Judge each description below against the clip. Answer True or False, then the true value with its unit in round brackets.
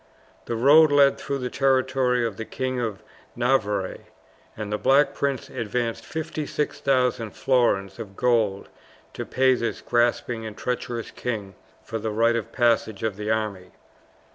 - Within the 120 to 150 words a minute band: True (145 wpm)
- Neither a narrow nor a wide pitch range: True (3.2 semitones)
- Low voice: True (120 Hz)